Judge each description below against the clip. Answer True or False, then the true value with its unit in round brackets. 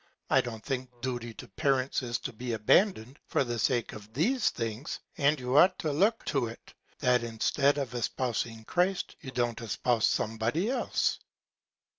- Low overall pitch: True (125 Hz)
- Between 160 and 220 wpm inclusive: True (170 wpm)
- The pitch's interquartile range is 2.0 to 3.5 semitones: False (4.0 semitones)